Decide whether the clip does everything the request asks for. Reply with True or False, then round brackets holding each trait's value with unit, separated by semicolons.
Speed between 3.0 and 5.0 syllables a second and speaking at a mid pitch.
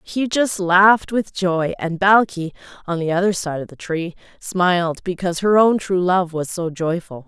True (4.6 syllables/s; 180 Hz)